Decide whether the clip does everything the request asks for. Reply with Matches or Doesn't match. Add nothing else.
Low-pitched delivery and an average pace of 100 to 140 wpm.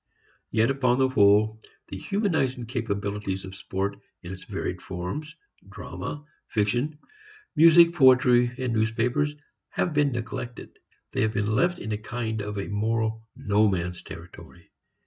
Matches